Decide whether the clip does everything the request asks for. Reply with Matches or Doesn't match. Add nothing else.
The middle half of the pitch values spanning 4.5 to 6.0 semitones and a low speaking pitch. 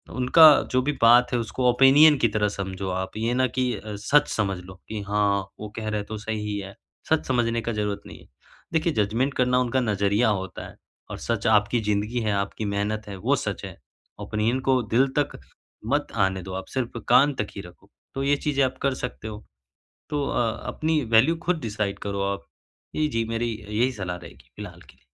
Doesn't match